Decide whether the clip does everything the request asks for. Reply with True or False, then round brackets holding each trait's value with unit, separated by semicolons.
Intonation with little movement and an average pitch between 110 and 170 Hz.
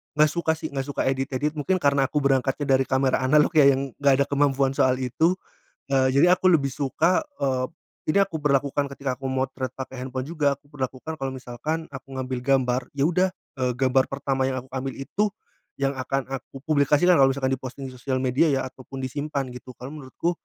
True (1.8 semitones; 135 Hz)